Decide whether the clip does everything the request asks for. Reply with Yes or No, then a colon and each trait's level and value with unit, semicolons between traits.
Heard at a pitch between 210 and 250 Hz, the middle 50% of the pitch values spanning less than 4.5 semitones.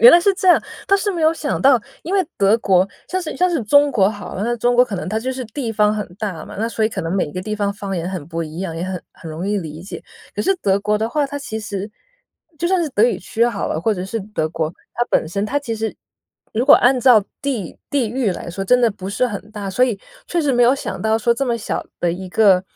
No: high, 220 Hz; average, 5.0 semitones